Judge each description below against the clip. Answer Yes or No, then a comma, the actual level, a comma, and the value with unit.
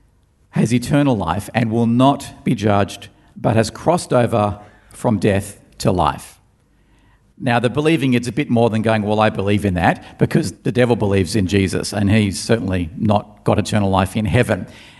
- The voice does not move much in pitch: No, average, 3.4 semitones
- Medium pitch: No, low, 110 Hz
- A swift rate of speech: No, average, 180 wpm